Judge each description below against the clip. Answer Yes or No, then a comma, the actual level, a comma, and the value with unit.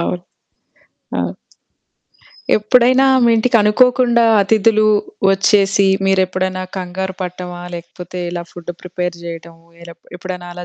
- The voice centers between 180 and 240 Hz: Yes, medium, 185 Hz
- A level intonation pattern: No, average, 3.3 semitones